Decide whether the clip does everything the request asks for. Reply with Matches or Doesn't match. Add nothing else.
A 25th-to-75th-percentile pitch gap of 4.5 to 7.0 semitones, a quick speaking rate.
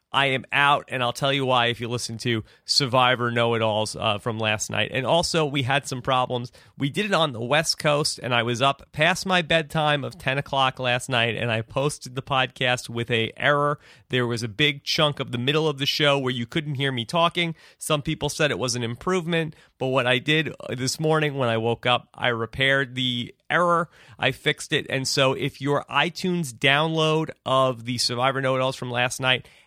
Doesn't match